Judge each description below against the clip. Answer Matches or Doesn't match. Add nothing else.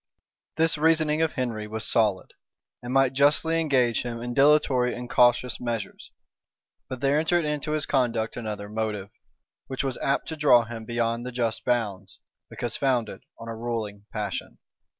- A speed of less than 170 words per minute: Matches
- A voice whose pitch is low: Matches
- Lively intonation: Doesn't match